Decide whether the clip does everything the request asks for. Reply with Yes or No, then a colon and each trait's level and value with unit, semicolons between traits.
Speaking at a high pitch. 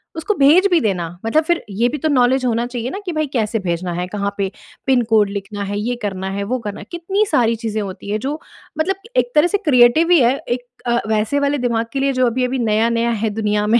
Yes: high, 235 Hz